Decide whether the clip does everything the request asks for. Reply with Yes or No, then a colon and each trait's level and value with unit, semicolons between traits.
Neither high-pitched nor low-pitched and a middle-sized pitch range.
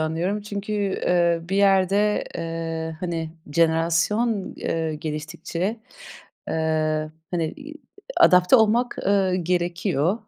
Yes: medium, 175 Hz; average, 3.7 semitones